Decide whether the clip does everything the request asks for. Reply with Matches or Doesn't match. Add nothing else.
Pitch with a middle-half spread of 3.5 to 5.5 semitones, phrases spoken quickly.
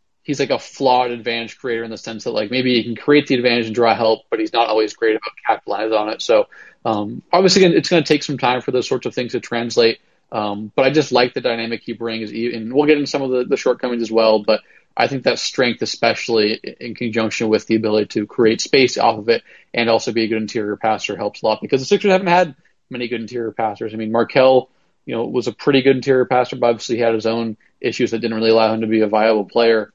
Doesn't match